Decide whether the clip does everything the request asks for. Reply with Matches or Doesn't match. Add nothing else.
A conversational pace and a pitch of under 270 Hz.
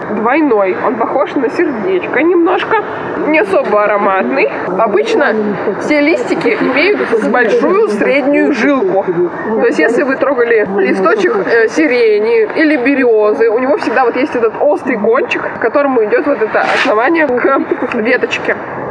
Doesn't match